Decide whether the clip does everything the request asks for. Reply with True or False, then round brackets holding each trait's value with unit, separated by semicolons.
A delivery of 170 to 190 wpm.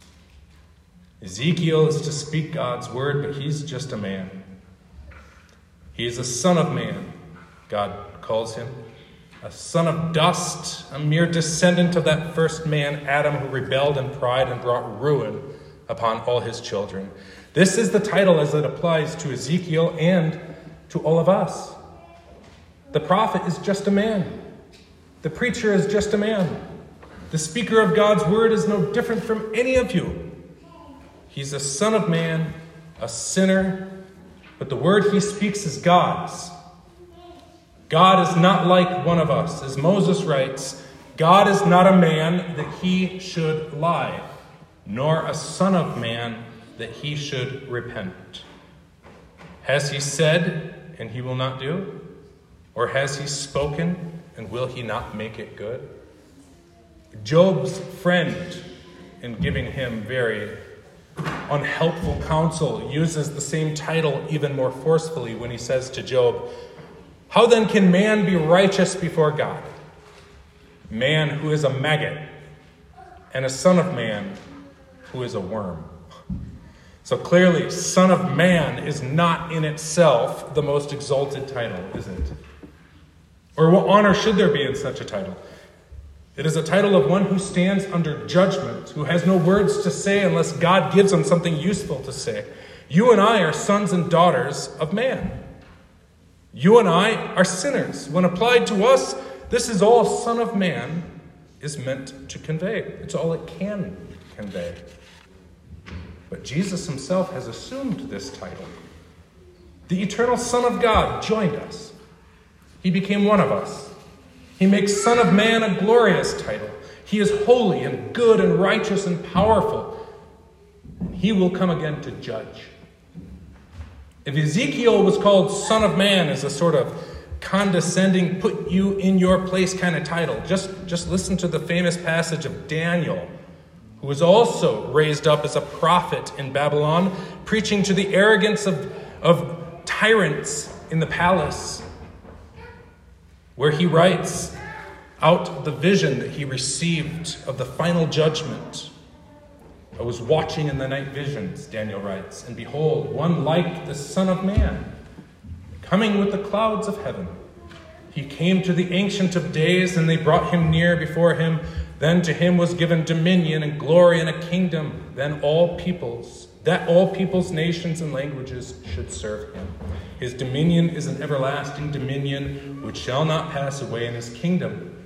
False (155 wpm)